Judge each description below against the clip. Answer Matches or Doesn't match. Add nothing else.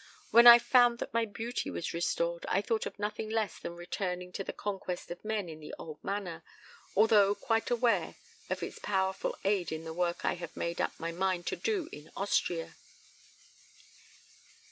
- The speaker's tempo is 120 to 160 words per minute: Doesn't match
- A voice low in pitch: Doesn't match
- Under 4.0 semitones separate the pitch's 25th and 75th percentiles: Doesn't match